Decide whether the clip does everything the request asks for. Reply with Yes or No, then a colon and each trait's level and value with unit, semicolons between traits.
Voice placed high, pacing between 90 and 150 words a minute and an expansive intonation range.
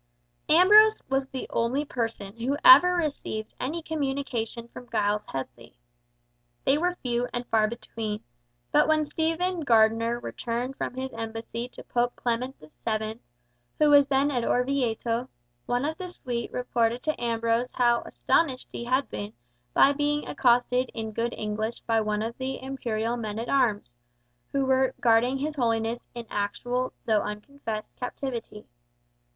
No: high, 245 Hz; average, 145 wpm; average, 3.1 semitones